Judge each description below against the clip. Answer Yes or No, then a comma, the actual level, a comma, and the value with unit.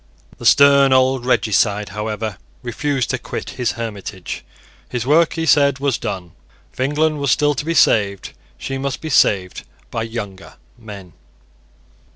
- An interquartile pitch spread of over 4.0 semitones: Yes, average, 5.1 semitones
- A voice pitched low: Yes, low, 125 Hz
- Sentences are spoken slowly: No, average, 150 wpm